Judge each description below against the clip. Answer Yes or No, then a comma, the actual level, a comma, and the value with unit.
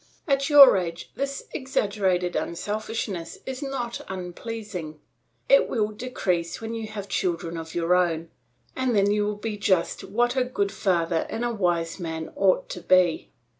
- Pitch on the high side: Yes, high, 200 Hz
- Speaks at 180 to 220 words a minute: No, average, 160 wpm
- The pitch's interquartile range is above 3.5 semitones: Yes, average, 5.1 semitones